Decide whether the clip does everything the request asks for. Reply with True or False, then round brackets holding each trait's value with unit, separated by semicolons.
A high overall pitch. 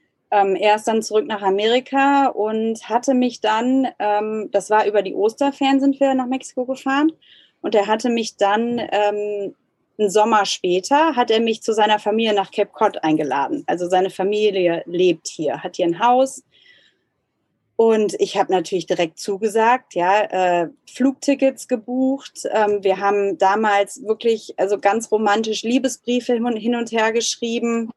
True (215 Hz)